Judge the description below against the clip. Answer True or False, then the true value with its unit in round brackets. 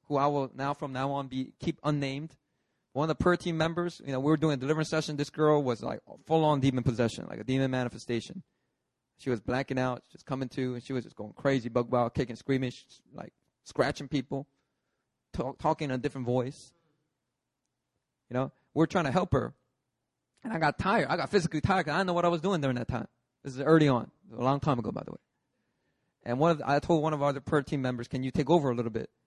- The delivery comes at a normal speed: False (250 wpm)